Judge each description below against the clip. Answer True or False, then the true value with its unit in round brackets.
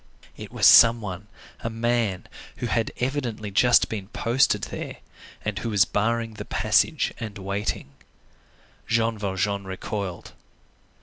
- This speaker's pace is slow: True (130 wpm)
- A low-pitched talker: True (110 Hz)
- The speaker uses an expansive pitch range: False (2.8 semitones)